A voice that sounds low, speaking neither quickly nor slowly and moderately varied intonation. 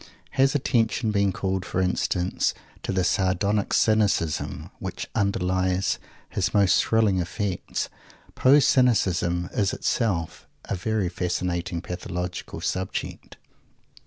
No: very low, 95 Hz; slow, 105 wpm; average, 3.1 semitones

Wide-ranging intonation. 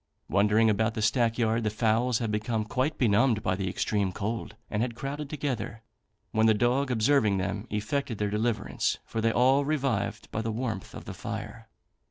No: average, 2.7 semitones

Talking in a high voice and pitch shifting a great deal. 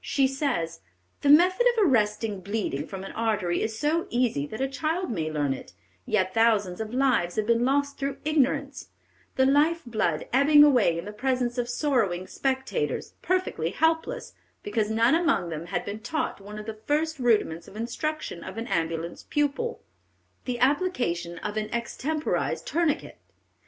Yes: high, 240 Hz; wide, 6.3 semitones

